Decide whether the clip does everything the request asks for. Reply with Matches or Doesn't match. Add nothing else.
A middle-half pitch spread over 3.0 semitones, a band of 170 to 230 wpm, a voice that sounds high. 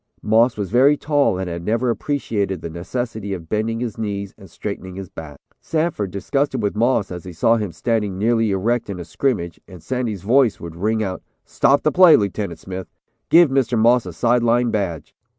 Doesn't match